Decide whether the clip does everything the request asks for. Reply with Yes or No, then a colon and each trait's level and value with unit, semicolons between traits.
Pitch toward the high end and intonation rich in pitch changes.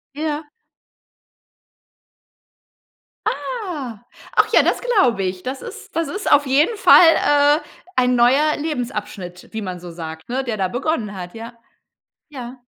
Yes: very high, 250 Hz; wide, 6.5 semitones